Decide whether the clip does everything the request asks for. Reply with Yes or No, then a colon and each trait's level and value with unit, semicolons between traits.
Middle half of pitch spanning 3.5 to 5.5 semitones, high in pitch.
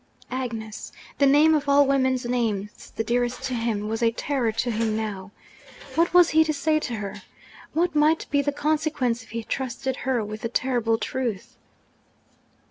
Yes: average, 4.2 semitones; very high, 250 Hz